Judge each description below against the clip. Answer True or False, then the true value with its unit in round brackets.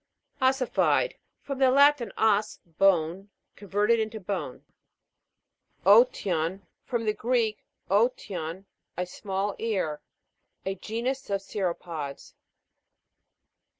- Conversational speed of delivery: False (90 wpm)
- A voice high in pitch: True (205 Hz)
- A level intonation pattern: False (4.2 semitones)